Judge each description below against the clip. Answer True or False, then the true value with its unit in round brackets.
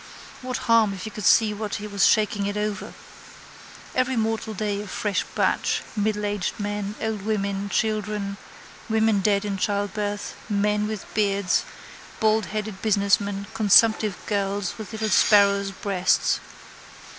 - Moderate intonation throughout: False (1.4 semitones)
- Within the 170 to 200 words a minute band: False (135 wpm)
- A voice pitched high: True (205 Hz)